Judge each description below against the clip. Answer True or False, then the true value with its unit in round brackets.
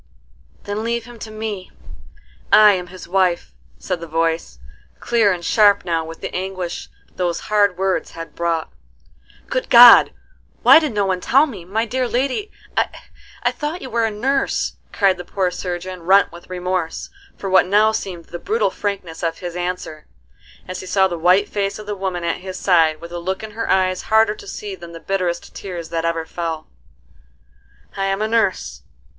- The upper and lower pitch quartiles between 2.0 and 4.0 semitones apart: True (3.6 semitones)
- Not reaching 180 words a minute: False (185 wpm)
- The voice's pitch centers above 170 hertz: True (190 Hz)